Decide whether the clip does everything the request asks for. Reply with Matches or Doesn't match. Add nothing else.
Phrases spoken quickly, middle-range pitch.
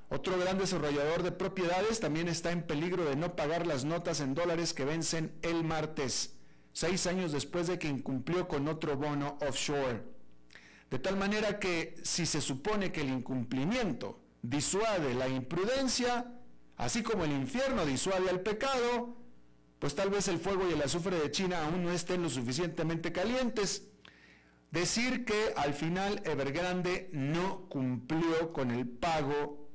Doesn't match